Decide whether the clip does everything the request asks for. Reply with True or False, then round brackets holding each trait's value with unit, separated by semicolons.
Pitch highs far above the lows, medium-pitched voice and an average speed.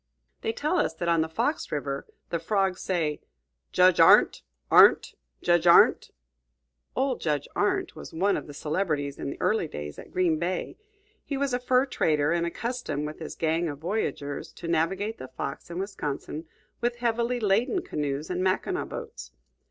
True (6.7 semitones; 175 Hz; 170 wpm)